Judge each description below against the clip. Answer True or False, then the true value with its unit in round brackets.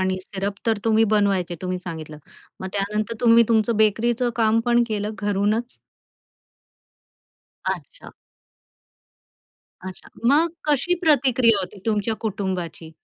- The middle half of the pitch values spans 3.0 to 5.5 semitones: True (3.3 semitones)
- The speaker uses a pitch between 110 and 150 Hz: False (215 Hz)